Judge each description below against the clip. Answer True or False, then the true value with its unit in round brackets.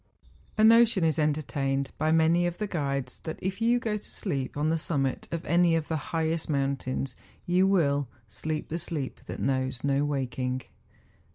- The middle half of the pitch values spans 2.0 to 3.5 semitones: False (4.0 semitones)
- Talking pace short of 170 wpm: False (180 wpm)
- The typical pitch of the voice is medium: True (155 Hz)